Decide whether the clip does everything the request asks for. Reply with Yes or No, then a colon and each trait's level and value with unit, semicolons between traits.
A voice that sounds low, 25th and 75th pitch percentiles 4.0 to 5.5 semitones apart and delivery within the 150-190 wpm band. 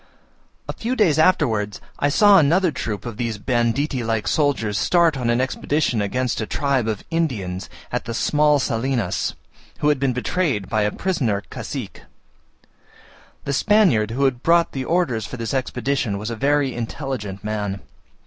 Yes: low, 130 Hz; average, 5.1 semitones; average, 160 wpm